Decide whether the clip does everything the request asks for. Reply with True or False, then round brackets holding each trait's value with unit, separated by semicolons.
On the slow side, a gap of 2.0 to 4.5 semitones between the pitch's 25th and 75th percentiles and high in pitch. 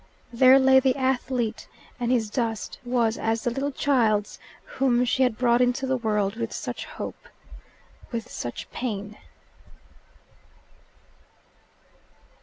True (120 wpm; 2.7 semitones; 240 Hz)